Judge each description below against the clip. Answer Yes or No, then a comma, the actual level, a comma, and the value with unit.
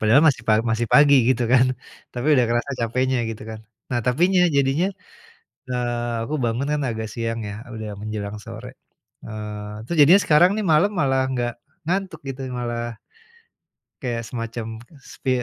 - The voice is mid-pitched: No, low, 120 Hz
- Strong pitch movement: No, average, 3.7 semitones